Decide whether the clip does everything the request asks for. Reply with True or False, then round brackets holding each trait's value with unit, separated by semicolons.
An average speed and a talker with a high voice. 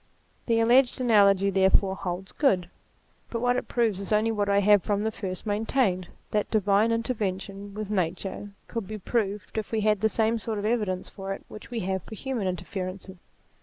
True (190 wpm; 205 Hz)